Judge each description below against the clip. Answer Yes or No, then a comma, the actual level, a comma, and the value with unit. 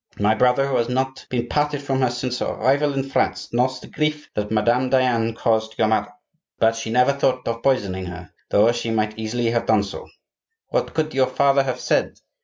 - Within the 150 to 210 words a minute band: Yes, fast, 205 wpm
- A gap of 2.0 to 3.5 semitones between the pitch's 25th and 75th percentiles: Yes, average, 3.0 semitones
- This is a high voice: No, low, 125 Hz